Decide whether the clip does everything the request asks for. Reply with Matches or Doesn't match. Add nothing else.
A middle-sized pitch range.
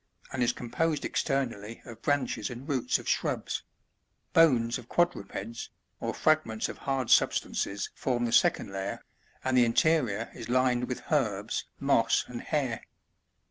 Matches